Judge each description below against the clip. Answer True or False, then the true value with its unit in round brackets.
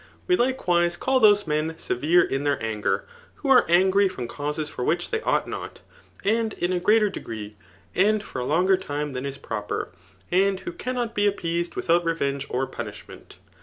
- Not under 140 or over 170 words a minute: False (180 wpm)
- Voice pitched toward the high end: False (175 Hz)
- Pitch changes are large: True (6.1 semitones)